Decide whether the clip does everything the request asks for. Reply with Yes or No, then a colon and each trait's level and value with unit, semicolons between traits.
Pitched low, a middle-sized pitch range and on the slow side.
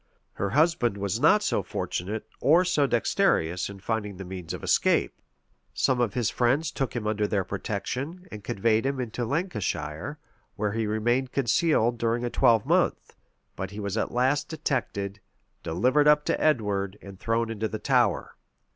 No: low, 115 Hz; average, 4.7 semitones; average, 165 wpm